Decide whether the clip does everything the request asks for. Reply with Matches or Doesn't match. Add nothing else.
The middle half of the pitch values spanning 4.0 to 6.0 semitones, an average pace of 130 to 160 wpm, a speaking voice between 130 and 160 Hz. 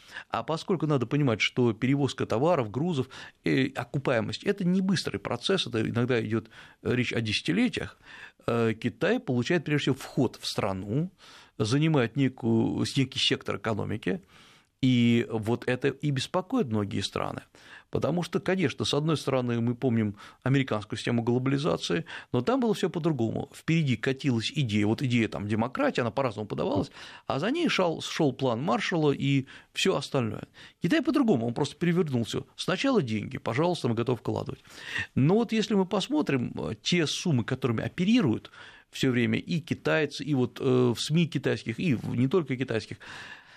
Matches